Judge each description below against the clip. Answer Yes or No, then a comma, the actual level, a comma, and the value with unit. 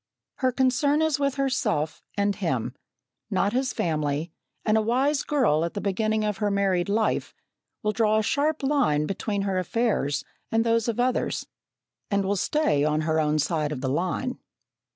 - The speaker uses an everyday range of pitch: No, wide, 7.6 semitones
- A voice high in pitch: Yes, high, 210 Hz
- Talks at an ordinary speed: Yes, average, 175 wpm